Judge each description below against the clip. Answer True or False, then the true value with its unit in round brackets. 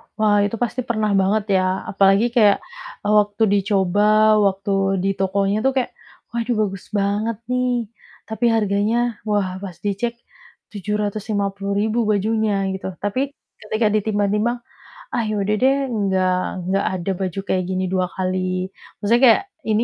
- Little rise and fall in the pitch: True (2.0 semitones)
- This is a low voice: False (205 Hz)